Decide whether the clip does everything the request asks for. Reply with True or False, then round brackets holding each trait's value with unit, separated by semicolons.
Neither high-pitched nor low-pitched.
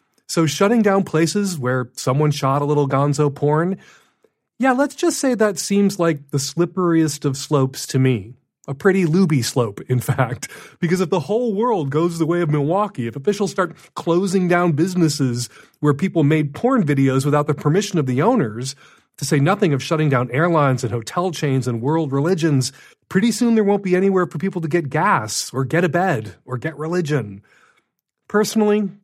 True (160 Hz)